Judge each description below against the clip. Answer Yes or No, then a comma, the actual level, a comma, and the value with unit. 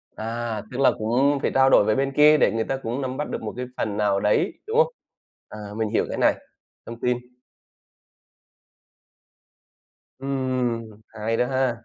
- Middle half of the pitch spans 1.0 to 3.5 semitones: Yes, average, 3.2 semitones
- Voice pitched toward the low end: Yes, low, 125 Hz